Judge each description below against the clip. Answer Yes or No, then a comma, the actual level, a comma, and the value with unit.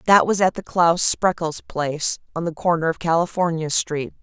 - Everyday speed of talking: Yes, average, 185 wpm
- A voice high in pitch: No, medium, 170 Hz